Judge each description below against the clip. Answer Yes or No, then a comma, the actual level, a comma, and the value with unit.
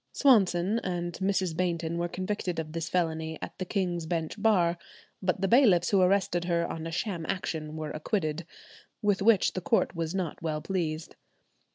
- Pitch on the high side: No, medium, 175 Hz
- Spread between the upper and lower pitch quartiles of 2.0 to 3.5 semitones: Yes, average, 2.8 semitones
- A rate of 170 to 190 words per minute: Yes, average, 175 wpm